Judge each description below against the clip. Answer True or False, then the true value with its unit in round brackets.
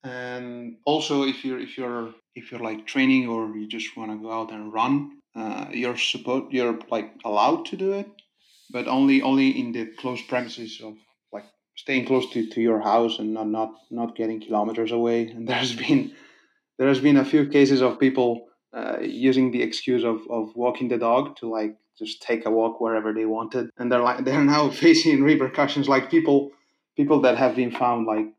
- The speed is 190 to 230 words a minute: True (200 wpm)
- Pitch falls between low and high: False (125 Hz)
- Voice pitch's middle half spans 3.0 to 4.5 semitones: True (3.6 semitones)